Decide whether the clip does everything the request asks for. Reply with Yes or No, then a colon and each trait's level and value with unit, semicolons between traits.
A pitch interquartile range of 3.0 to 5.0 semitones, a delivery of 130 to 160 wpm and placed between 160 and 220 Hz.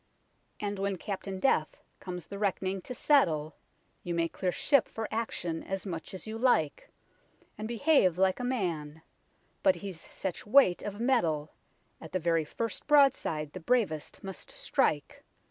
No: wide, 5.5 semitones; average, 155 wpm; high, 190 Hz